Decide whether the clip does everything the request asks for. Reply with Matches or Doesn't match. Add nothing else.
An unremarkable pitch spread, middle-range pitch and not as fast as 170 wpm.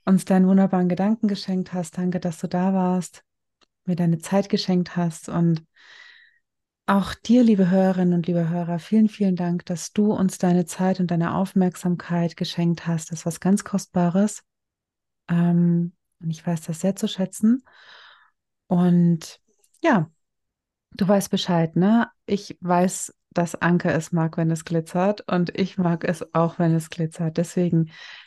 Doesn't match